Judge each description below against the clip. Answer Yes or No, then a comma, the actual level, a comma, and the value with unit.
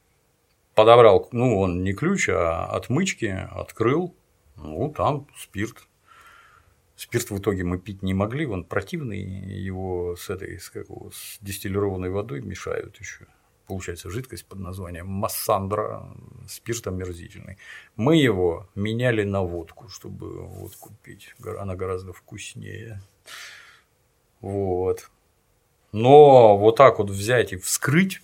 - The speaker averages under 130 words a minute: Yes, average, 115 wpm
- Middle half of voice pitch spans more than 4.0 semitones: No, average, 3.6 semitones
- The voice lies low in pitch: Yes, low, 100 Hz